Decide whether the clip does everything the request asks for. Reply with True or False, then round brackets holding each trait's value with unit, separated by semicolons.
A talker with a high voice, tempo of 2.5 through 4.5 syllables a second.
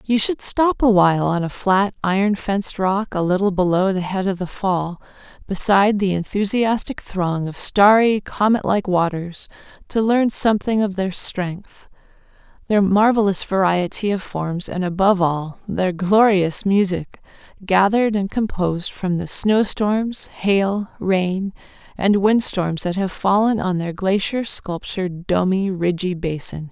True (195 Hz; 4.2 syllables/s)